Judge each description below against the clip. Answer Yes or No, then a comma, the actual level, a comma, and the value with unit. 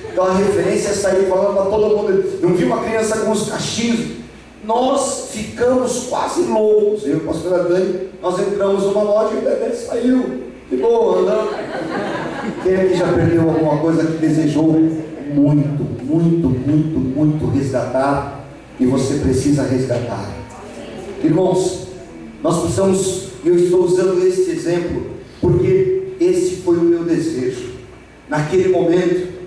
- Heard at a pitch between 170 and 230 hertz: Yes, medium, 185 Hz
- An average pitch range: No, wide, 6.4 semitones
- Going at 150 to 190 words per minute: No, average, 135 wpm